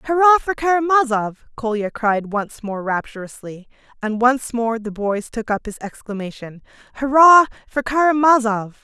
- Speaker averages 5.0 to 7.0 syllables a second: No, 4.7 syllables/s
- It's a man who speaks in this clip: No, female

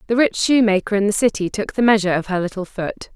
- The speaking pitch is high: Yes, high, 210 Hz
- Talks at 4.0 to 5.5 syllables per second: No, 6.5 syllables/s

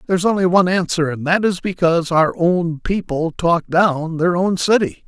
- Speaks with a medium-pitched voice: Yes, medium, 170 Hz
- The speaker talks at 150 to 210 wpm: Yes, average, 200 wpm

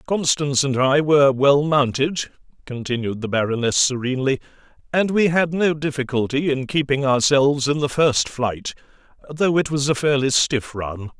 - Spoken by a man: Yes, male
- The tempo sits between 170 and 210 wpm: No, average, 155 wpm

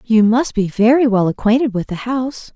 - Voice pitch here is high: Yes, high, 230 Hz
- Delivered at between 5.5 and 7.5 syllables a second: No, 5.3 syllables/s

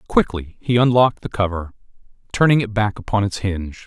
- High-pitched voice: No, low, 105 Hz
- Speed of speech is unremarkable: Yes, average, 170 wpm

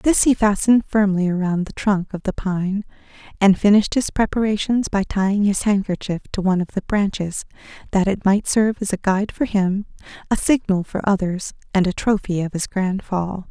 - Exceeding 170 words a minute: Yes, average, 190 wpm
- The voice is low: No, high, 200 Hz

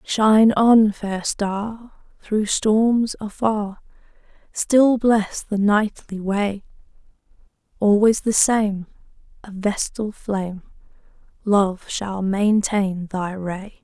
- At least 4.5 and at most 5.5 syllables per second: No, 2.9 syllables/s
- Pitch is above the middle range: Yes, high, 205 Hz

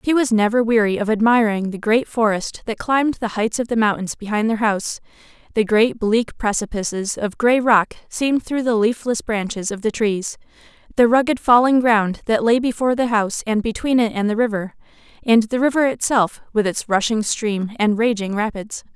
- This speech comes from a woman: Yes, female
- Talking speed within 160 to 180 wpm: No, average, 190 wpm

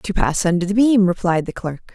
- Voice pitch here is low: No, high, 190 Hz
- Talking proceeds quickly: Yes, fast, 245 wpm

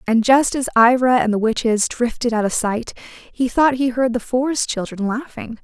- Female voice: Yes, female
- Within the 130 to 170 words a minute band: No, average, 200 wpm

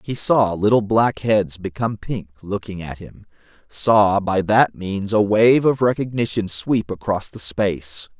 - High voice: No, low, 105 Hz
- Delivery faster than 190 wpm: No, average, 160 wpm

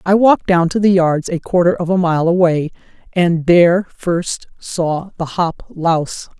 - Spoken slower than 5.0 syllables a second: Yes, 4.4 syllables/s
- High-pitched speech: No, medium, 175 Hz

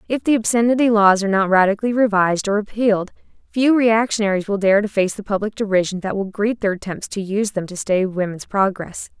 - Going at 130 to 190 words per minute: No, average, 200 wpm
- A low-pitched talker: No, high, 205 Hz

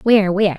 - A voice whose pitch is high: Yes, high, 200 Hz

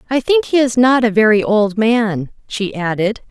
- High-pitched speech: Yes, high, 225 Hz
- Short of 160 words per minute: No, average, 200 wpm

